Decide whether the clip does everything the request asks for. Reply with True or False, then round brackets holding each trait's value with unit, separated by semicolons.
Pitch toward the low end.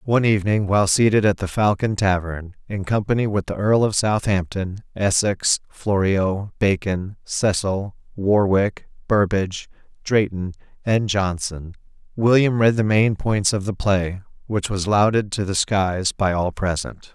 True (100 Hz)